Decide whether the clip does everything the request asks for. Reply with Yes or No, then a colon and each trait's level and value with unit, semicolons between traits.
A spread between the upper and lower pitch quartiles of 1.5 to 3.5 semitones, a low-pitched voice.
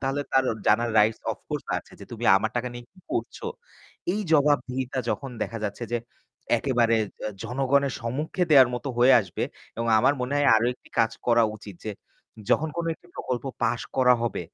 Yes: average, 3.1 semitones; low, 125 Hz